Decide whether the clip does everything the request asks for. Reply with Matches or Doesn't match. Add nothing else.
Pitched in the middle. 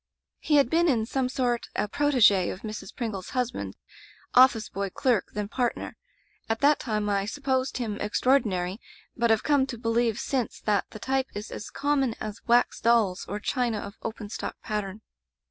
Doesn't match